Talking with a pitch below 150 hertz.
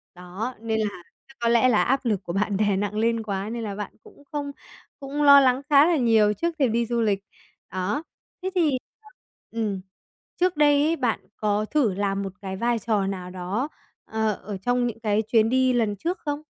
No: high, 225 Hz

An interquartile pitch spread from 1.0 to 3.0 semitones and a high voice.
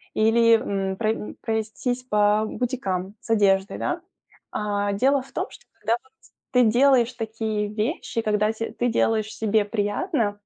Yes: narrow, 2.4 semitones; high, 220 Hz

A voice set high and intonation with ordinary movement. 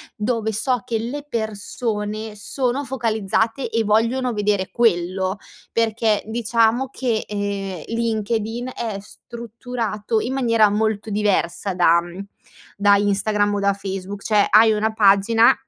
No: high, 215 Hz; narrow, 2.2 semitones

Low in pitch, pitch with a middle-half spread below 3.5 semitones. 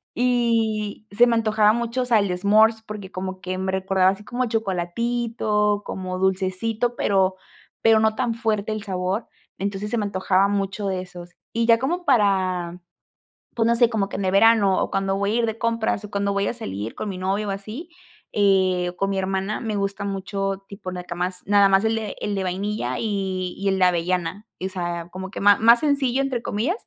No: high, 200 Hz; average, 3.0 semitones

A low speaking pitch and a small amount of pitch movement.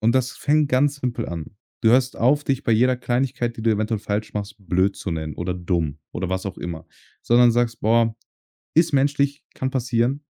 No: low, 115 Hz; average, 4.7 semitones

